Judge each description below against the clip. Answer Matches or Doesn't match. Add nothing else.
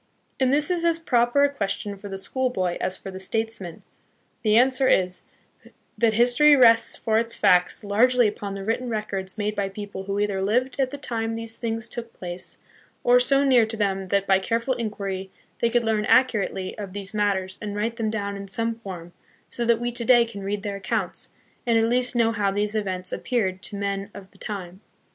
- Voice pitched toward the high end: Matches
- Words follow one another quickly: Matches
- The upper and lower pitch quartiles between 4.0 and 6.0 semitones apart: Doesn't match